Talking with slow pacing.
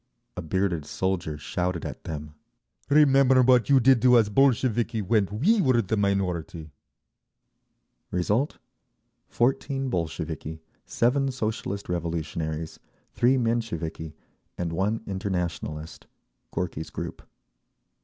Yes: slow, 100 wpm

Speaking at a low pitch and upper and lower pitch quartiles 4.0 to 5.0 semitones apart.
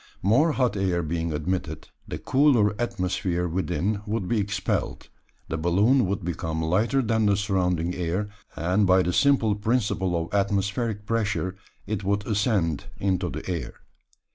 No: low, 100 Hz; average, 3.4 semitones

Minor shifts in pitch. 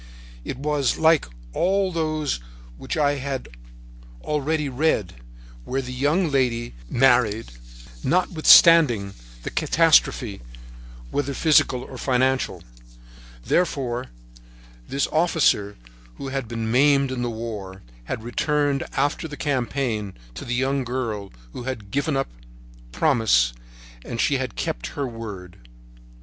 No: average, 4.2 semitones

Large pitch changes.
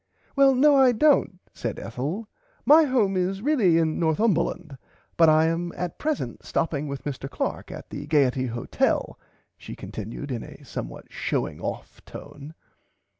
Yes: wide, 8.6 semitones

